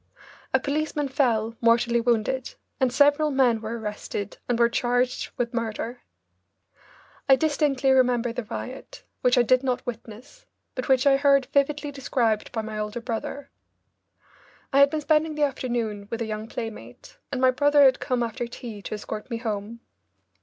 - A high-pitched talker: Yes, high, 245 Hz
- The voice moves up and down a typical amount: Yes, average, 3.1 semitones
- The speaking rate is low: No, average, 165 wpm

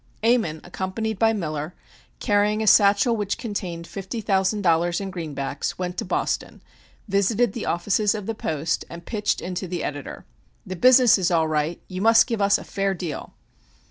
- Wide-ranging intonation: No, average, 3.8 semitones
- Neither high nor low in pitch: No, high, 195 Hz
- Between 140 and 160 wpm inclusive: No, average, 175 wpm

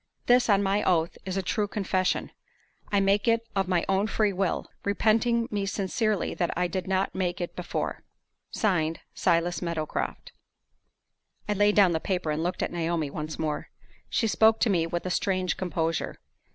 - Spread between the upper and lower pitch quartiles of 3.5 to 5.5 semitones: No, average, 3.1 semitones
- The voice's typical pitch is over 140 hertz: Yes, high, 190 Hz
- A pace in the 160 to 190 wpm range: Yes, average, 175 wpm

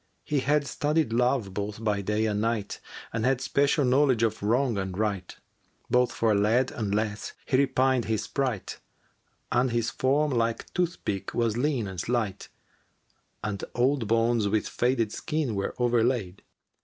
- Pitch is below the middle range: Yes, low, 115 Hz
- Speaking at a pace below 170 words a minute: Yes, average, 160 wpm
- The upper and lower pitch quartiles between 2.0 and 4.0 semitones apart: Yes, average, 3.7 semitones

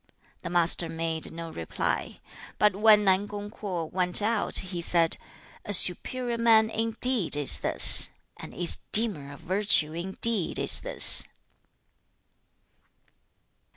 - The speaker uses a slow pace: Yes, slow, 120 wpm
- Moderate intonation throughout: Yes, average, 4.6 semitones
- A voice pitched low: No, high, 190 Hz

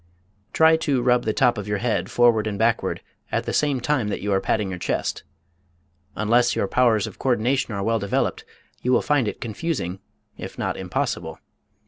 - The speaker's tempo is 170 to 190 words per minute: Yes, average, 185 wpm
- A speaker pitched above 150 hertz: No, low, 115 Hz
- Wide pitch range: No, average, 3.5 semitones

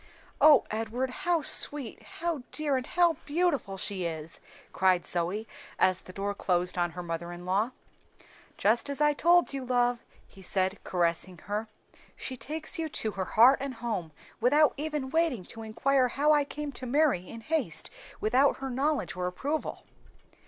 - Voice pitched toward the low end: No, high, 245 Hz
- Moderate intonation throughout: No, wide, 7.6 semitones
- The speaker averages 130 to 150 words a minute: No, average, 165 wpm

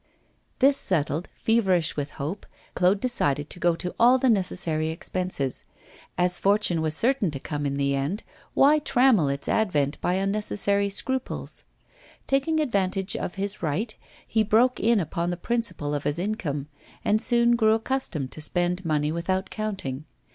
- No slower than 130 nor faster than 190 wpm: Yes, average, 155 wpm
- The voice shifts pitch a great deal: Yes, wide, 6.0 semitones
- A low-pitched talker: No, medium, 185 Hz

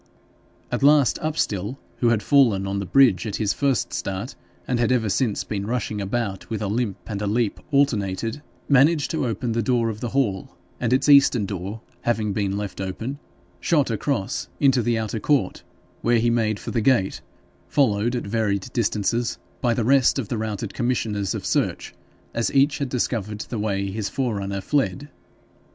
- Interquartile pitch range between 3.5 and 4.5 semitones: Yes, average, 4.1 semitones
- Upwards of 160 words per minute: Yes, average, 180 wpm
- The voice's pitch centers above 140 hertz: No, low, 115 Hz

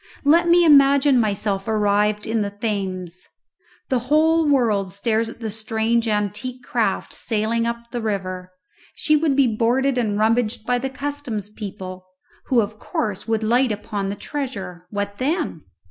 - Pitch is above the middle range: Yes, high, 225 Hz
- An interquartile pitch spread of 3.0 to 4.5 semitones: Yes, average, 4.0 semitones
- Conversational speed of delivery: Yes, average, 155 wpm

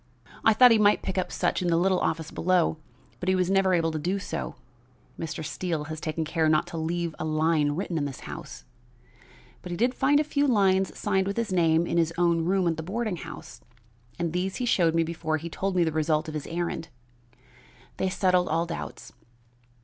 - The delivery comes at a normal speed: No, fast, 215 wpm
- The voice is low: No, medium, 170 Hz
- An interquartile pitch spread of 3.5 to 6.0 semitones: No, average, 2.9 semitones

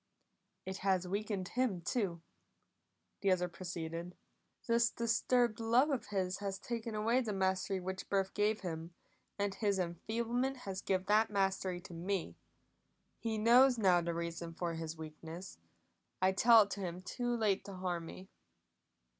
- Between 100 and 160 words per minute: Yes, average, 155 wpm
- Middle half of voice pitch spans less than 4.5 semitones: Yes, average, 3.7 semitones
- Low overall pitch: No, high, 195 Hz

